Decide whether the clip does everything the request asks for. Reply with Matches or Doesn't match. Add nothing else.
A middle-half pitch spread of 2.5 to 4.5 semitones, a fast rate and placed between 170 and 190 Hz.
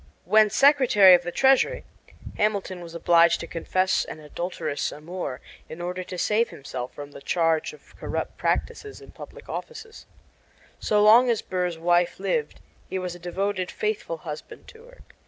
Doesn't match